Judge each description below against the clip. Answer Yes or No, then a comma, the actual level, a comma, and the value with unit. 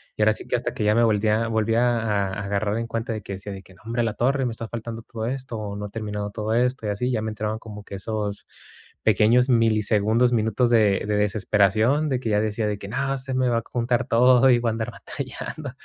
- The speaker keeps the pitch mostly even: Yes, narrow, 2.3 semitones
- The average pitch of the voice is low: Yes, low, 110 Hz